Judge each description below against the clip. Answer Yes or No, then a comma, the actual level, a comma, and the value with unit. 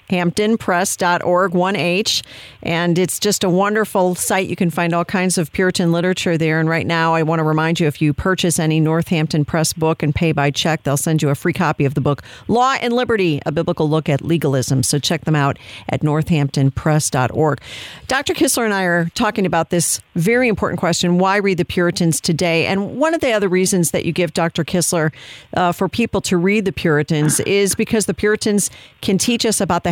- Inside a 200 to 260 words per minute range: Yes, fast, 205 wpm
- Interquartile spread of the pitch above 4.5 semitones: No, average, 3.5 semitones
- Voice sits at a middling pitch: Yes, medium, 175 Hz